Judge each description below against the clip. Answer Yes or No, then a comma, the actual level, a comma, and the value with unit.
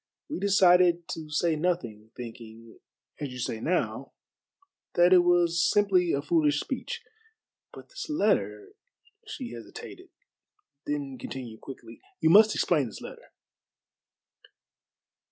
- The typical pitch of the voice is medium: Yes, medium, 165 Hz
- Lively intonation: Yes, wide, 6.2 semitones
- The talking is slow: Yes, slow, 120 wpm